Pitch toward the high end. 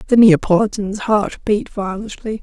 Yes: high, 205 Hz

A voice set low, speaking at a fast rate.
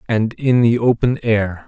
No: low, 115 Hz; average, 180 wpm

